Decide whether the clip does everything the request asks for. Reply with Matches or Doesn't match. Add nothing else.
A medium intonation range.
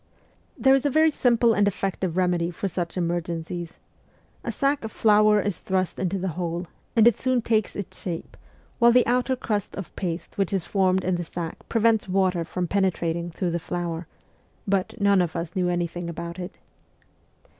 Matches